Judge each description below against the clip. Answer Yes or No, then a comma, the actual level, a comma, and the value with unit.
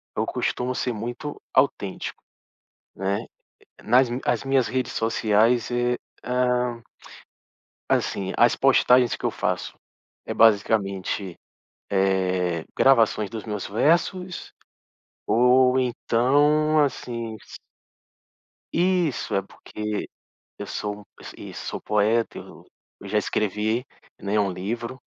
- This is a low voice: Yes, low, 115 Hz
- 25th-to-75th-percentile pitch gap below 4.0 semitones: Yes, average, 3.6 semitones